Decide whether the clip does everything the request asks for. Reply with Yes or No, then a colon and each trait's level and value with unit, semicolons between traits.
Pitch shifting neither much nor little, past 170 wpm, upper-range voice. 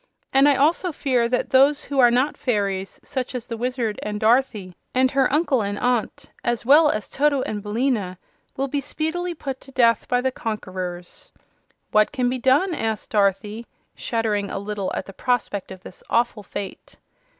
Yes: average, 4.6 semitones; average, 180 wpm; high, 245 Hz